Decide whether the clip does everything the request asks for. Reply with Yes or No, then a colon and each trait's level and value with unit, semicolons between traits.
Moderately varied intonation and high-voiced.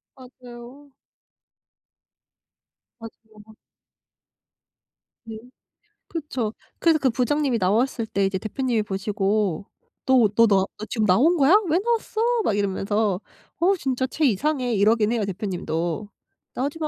Yes: average, 4.8 semitones; high, 230 Hz